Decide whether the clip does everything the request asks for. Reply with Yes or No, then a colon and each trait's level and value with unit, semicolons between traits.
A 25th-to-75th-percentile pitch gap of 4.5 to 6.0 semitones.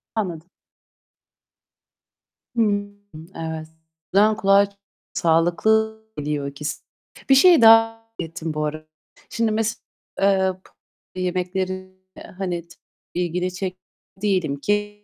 No: average, 3.7 semitones